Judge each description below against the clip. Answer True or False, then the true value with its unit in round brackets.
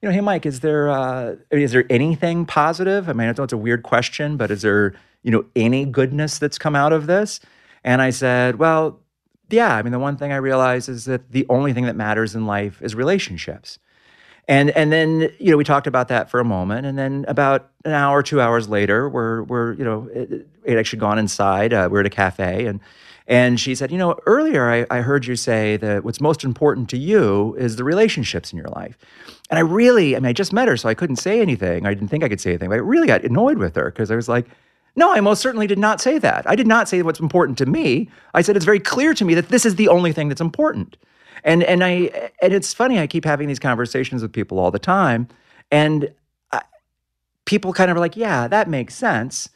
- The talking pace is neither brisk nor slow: False (245 wpm)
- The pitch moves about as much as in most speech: False (6.4 semitones)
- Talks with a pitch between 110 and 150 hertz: True (140 Hz)